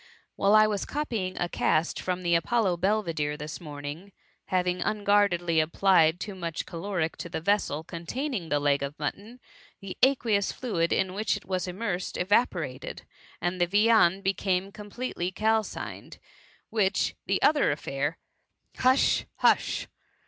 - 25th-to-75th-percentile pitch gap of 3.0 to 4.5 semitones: Yes, average, 3.9 semitones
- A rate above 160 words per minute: No, average, 155 wpm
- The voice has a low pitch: No, medium, 185 Hz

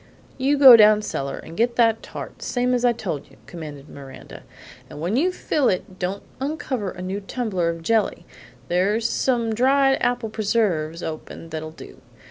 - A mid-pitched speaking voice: No, high, 210 Hz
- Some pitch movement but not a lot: No, wide, 6.5 semitones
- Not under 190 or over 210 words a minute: No, average, 170 wpm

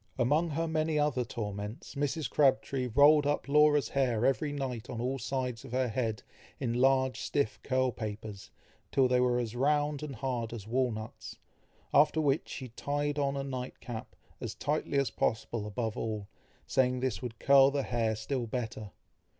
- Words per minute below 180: Yes, average, 170 wpm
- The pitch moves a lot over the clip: No, average, 3.7 semitones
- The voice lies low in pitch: Yes, low, 130 Hz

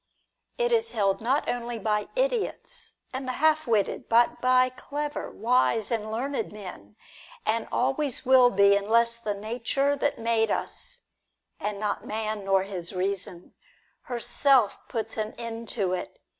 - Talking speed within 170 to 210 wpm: No, average, 155 wpm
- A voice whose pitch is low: No, high, 230 Hz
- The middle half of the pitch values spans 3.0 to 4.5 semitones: Yes, average, 4.0 semitones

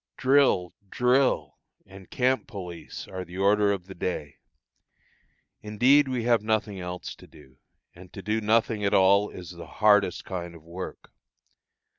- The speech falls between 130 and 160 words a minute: Yes, average, 150 wpm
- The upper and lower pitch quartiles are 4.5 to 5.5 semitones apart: No, average, 3.7 semitones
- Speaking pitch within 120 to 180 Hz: No, low, 100 Hz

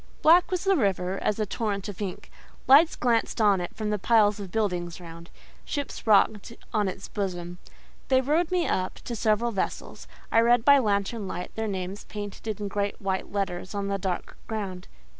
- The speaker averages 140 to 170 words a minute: No, average, 185 wpm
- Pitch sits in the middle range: No, high, 205 Hz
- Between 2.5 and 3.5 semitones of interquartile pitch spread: Yes, average, 3.2 semitones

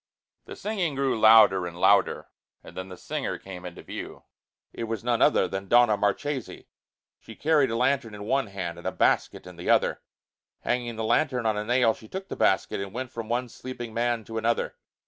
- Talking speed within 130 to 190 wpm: No, fast, 205 wpm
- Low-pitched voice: Yes, low, 115 Hz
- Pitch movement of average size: Yes, average, 3.8 semitones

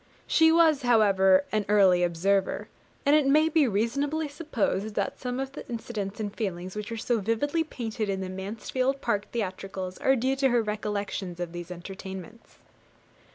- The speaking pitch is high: Yes, high, 215 Hz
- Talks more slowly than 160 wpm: No, average, 165 wpm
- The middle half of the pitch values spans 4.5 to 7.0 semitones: Yes, wide, 5.6 semitones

